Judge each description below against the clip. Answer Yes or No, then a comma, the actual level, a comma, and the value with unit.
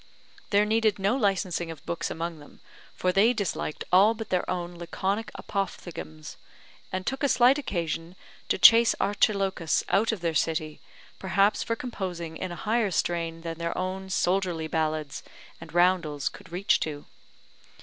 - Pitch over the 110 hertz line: Yes, medium, 185 Hz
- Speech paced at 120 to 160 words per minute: Yes, average, 155 wpm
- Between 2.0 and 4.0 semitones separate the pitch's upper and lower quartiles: Yes, average, 3.6 semitones